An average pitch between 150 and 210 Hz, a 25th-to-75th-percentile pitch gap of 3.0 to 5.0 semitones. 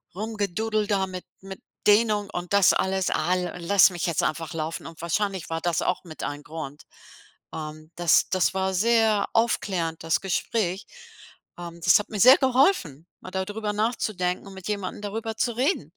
Yes: high, 190 Hz; average, 3.9 semitones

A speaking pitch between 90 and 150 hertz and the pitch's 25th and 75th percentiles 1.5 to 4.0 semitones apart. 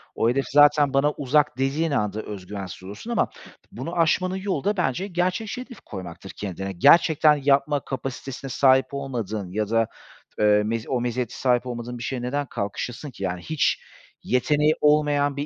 No: low, 135 Hz; average, 5.3 semitones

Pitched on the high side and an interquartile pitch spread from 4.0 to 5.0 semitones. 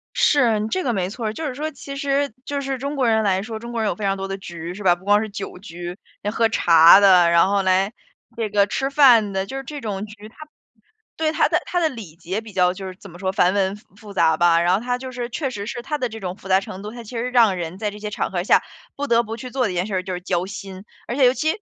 Yes: high, 210 Hz; average, 4.6 semitones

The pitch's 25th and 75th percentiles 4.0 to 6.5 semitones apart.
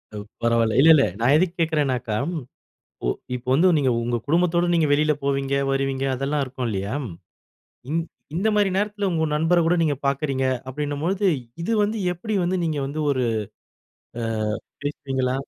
Yes: average, 4.4 semitones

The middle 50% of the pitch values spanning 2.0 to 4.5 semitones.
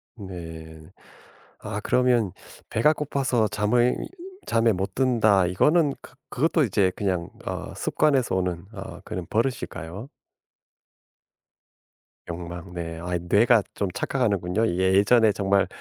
No: average, 5.3 semitones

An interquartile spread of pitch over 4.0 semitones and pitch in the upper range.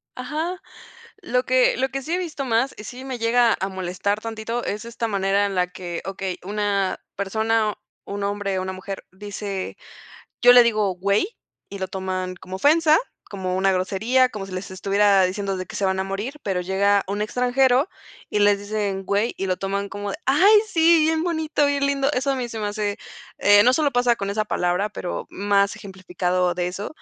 Yes: average, 4.4 semitones; high, 205 Hz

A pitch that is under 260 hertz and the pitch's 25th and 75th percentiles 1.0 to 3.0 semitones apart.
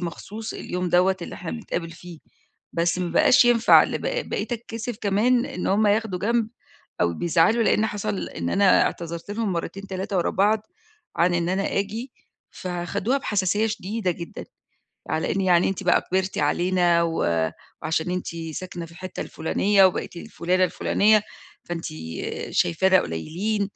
No: high, 190 Hz; average, 3.5 semitones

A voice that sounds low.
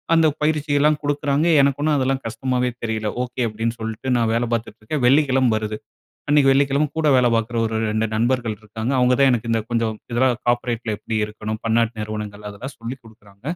Yes: low, 120 Hz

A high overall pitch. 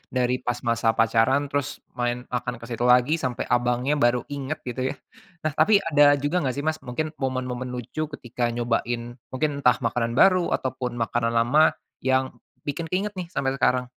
No: low, 125 Hz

